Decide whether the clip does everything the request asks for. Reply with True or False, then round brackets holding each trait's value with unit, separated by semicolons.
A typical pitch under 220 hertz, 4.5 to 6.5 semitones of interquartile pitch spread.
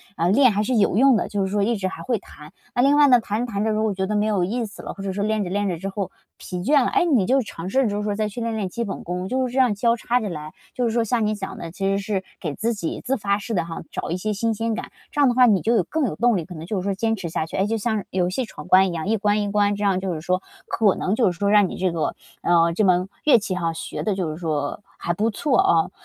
False (205 Hz; 3.7 semitones)